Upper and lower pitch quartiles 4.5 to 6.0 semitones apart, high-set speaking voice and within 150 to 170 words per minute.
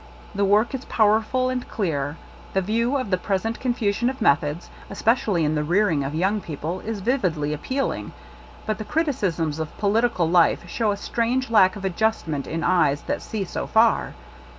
No: wide, 5.6 semitones; high, 200 Hz; average, 180 wpm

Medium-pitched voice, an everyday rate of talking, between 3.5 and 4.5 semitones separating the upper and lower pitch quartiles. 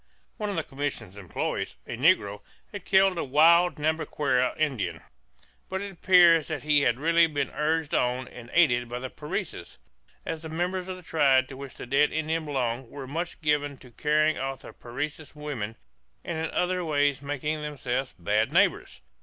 Yes: medium, 150 Hz; average, 180 wpm; average, 3.8 semitones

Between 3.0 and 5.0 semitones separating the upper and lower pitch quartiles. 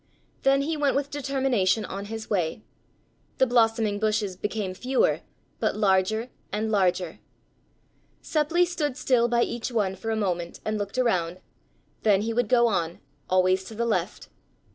Yes: average, 4.6 semitones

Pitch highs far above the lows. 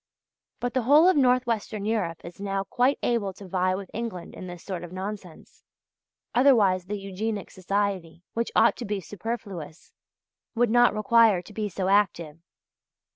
No: average, 3.9 semitones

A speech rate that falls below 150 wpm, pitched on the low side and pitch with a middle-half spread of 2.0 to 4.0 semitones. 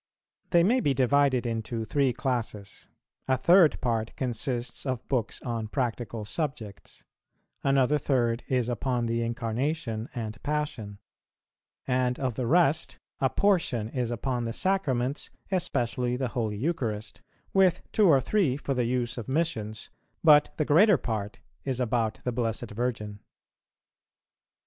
Yes: slow, 135 wpm; low, 125 Hz; average, 3.7 semitones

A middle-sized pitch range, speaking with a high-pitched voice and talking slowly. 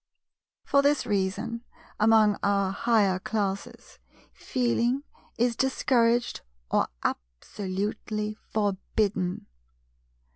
Yes: average, 3.2 semitones; high, 215 Hz; slow, 75 wpm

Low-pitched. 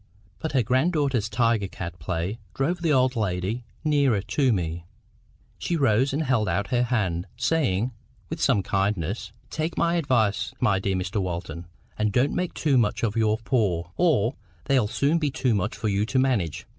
Yes: low, 115 Hz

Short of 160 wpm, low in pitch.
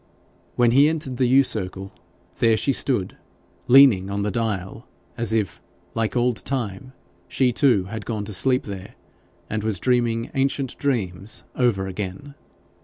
Yes: average, 150 wpm; low, 115 Hz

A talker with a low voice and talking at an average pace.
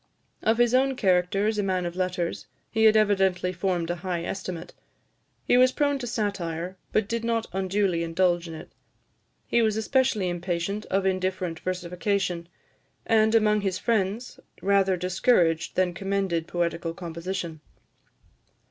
No: high, 190 Hz; average, 145 wpm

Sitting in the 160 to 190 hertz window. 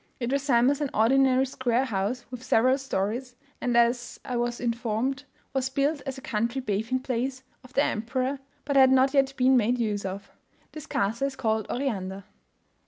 No: very high, 250 Hz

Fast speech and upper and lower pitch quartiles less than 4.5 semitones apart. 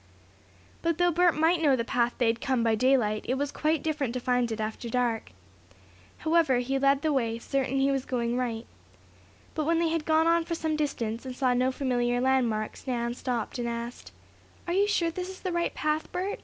No: fast, 215 wpm; average, 4.8 semitones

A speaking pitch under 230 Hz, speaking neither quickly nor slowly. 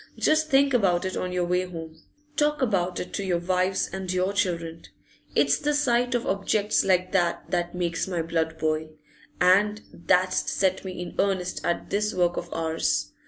Yes: medium, 185 Hz; average, 180 wpm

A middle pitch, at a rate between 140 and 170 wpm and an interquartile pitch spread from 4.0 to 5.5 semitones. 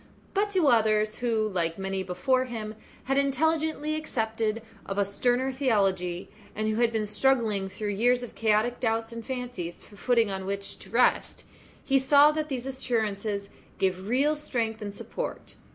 No: high, 225 Hz; average, 165 wpm; average, 4.3 semitones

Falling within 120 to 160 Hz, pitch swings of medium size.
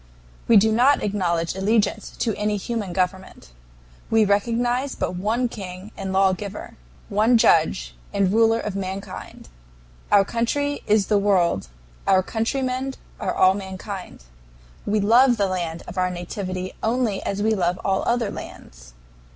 No: high, 200 Hz; average, 3.4 semitones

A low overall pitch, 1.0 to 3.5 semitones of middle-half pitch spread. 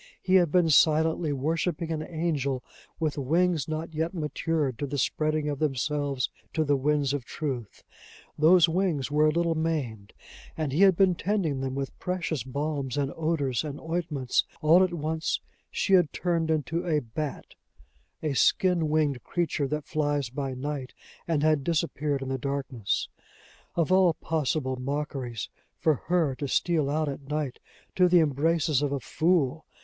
No: medium, 150 Hz; average, 2.9 semitones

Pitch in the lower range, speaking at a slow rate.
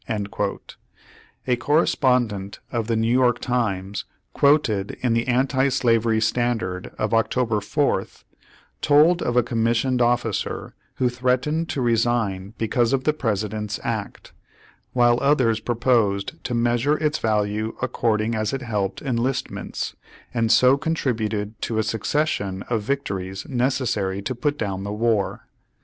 Yes: low, 120 Hz; slow, 130 wpm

